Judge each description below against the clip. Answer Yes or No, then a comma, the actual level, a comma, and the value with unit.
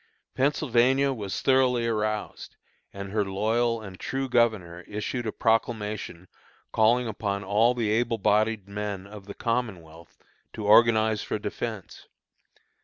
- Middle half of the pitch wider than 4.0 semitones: No, narrow, 2.6 semitones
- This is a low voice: Yes, low, 110 Hz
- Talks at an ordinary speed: No, slow, 125 wpm